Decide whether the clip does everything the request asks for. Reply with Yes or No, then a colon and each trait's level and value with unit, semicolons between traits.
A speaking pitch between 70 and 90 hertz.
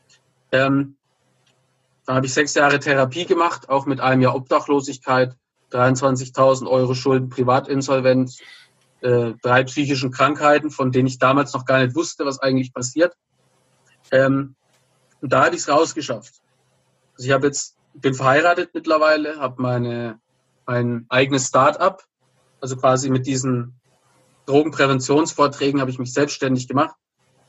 No: low, 135 Hz